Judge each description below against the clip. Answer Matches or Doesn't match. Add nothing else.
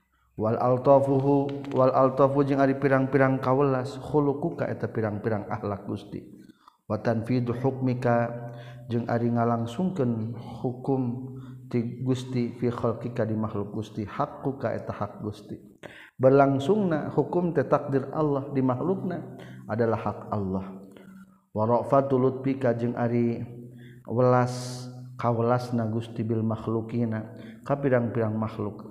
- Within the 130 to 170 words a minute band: Doesn't match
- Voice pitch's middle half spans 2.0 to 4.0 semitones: Matches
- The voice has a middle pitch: Doesn't match